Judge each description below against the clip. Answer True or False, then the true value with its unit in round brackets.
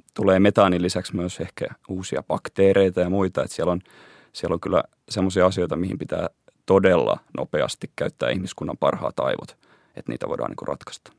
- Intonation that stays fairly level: True (1.4 semitones)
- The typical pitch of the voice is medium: False (95 Hz)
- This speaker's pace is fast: True (165 wpm)